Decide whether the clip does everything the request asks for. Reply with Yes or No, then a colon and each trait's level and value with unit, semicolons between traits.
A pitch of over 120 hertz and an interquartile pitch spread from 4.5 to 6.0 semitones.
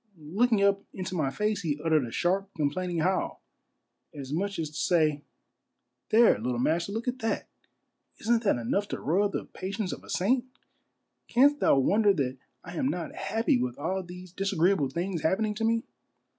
Yes: medium, 185 Hz; average, 5.2 semitones